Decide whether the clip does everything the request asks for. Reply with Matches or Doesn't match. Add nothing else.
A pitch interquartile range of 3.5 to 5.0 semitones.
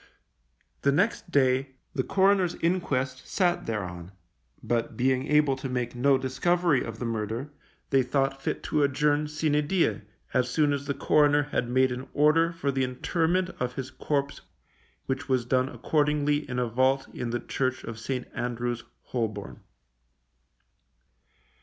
Doesn't match